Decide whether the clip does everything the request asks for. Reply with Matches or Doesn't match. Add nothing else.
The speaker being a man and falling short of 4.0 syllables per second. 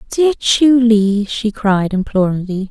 Doesn't match